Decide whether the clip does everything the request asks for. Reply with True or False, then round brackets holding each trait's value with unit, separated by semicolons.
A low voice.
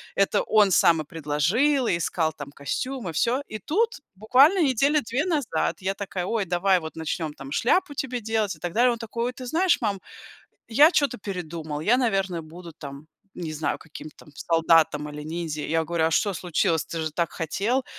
False (185 Hz)